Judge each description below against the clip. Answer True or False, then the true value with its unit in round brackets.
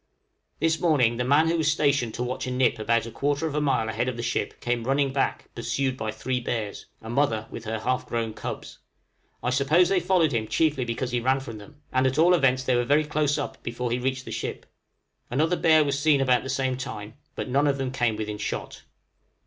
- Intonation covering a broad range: False (3.6 semitones)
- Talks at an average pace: False (230 wpm)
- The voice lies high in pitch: False (130 Hz)